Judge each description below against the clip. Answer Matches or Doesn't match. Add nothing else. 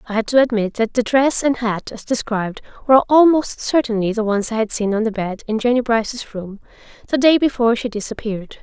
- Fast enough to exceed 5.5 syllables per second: Matches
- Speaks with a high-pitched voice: Matches